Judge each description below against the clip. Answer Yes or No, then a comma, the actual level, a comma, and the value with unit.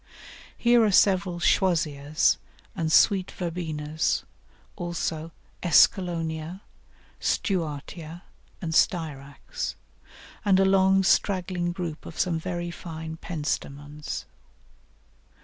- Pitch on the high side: No, medium, 170 Hz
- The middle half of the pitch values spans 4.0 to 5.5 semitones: No, average, 2.8 semitones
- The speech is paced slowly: Yes, slow, 85 wpm